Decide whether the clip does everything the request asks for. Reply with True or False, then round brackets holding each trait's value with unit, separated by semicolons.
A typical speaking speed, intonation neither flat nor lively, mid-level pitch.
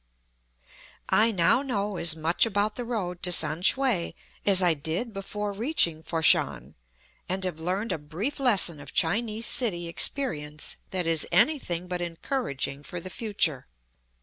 True (150 wpm; 5.0 semitones; 180 Hz)